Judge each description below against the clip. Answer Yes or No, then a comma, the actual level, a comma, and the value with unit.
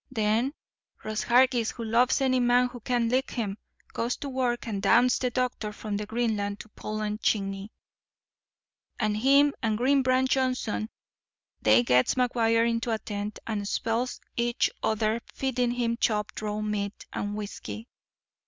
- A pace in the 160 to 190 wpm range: No, average, 150 wpm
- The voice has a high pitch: Yes, high, 230 Hz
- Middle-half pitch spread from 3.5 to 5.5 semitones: No, average, 3.0 semitones